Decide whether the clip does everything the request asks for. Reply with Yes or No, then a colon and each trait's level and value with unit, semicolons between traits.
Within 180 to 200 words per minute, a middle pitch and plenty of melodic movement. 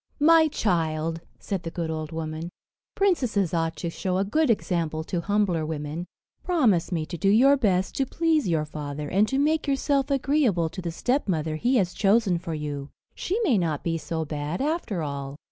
Yes: average, 185 wpm; medium, 175 Hz; wide, 7.5 semitones